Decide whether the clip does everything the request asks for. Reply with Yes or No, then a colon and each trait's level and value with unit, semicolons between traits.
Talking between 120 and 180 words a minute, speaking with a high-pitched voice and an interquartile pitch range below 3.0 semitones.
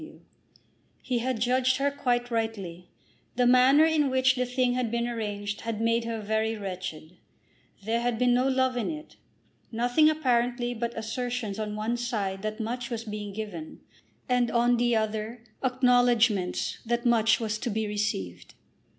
Yes: average, 160 wpm; high, 235 Hz; narrow, 2.5 semitones